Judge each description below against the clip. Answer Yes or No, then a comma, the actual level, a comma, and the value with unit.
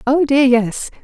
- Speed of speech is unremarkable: Yes, average, 175 wpm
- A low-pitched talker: No, very high, 265 Hz